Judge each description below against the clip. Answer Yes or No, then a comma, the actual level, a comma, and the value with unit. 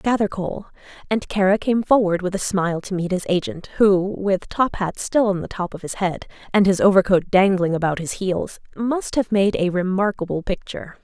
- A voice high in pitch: Yes, high, 195 Hz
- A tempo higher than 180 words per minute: Yes, average, 195 wpm